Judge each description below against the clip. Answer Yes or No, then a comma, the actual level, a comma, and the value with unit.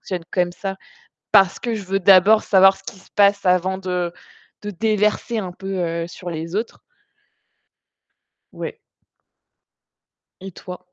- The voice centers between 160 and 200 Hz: Yes, high, 190 Hz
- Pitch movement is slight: Yes, narrow, 1.9 semitones